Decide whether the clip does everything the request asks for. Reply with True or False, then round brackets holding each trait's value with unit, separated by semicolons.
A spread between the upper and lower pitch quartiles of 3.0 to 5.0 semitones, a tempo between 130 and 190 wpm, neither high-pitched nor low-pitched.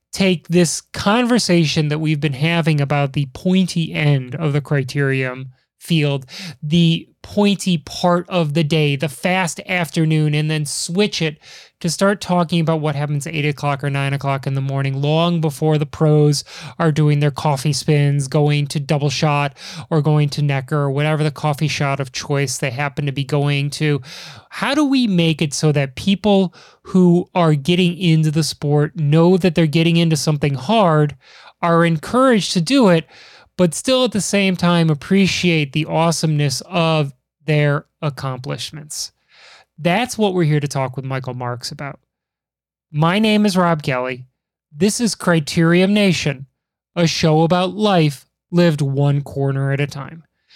True (3.3 semitones; 165 wpm; 155 Hz)